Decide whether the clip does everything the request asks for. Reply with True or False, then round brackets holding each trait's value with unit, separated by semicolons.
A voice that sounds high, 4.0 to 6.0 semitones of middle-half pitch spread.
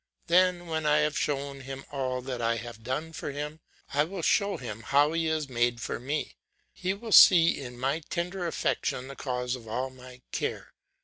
False (140 Hz; 4.3 semitones)